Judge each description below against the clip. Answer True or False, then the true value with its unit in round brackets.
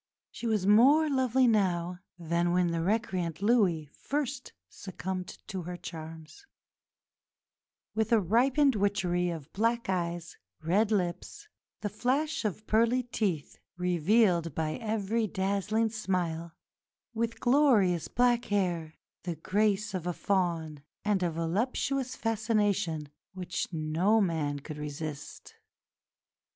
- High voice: True (195 Hz)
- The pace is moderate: False (115 wpm)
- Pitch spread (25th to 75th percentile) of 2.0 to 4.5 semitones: False (5.0 semitones)